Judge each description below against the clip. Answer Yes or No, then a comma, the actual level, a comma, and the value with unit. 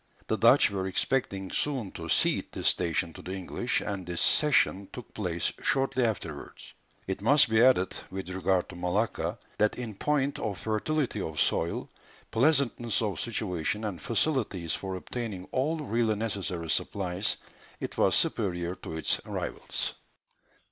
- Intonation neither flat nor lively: Yes, average, 4.7 semitones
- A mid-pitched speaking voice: No, low, 100 Hz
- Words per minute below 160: Yes, average, 150 wpm